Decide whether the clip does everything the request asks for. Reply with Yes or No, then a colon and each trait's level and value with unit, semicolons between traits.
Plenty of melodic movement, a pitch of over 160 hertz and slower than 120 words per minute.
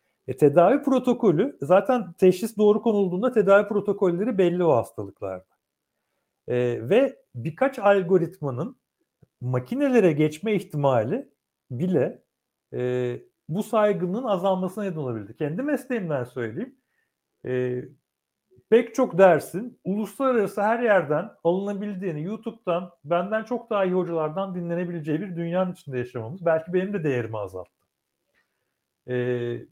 Yes: wide, 6.2 semitones; medium, 185 Hz; average, 105 wpm